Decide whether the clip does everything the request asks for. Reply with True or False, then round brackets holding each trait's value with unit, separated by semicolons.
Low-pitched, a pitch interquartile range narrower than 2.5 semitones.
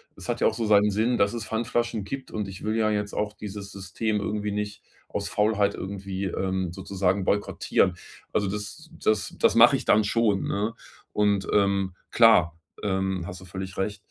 True (100 Hz; 1.8 semitones)